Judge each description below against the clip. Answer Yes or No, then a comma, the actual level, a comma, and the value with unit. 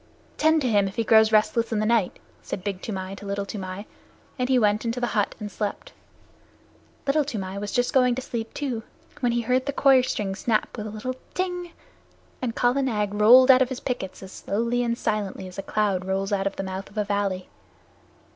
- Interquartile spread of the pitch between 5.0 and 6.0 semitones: No, average, 3.8 semitones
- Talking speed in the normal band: No, fast, 220 wpm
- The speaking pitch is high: Yes, high, 215 Hz